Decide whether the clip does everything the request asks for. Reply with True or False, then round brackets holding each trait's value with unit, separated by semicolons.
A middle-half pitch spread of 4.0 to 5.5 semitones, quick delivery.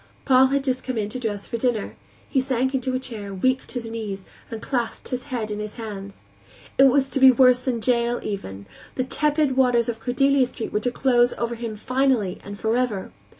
False (3.1 semitones; 210 wpm)